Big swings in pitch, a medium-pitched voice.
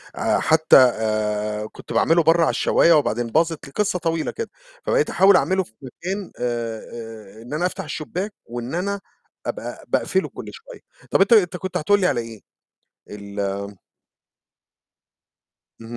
Yes: wide, 8.4 semitones; medium, 155 Hz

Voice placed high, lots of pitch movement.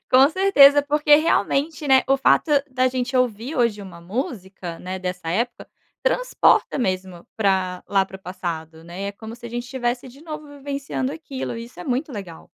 Yes: high, 240 Hz; wide, 6.6 semitones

